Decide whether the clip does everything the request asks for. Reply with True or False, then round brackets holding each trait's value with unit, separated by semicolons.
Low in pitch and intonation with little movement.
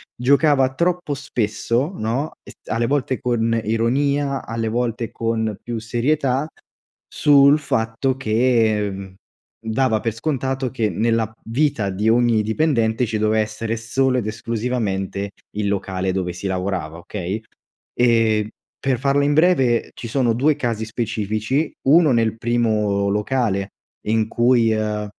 False (115 Hz; 3.5 semitones)